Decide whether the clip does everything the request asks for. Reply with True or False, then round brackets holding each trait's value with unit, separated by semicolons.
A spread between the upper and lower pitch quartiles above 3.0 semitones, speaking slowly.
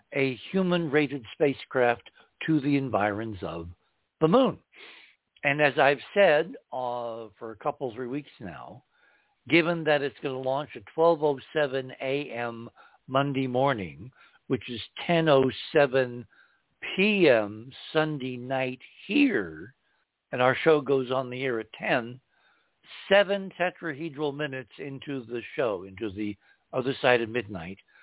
True (3.8 semitones; 125 wpm)